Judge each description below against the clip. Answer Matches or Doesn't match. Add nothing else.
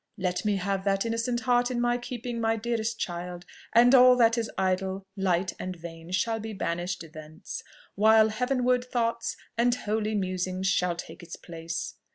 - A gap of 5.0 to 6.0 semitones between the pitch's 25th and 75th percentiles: Doesn't match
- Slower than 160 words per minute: Doesn't match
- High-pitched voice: Matches